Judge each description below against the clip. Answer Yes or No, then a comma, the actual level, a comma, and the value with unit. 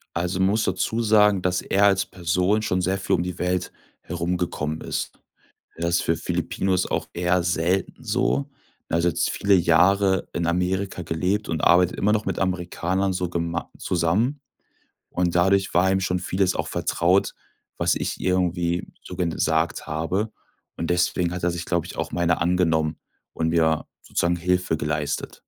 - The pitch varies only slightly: Yes, narrow, 1.9 semitones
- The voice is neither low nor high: No, very low, 90 Hz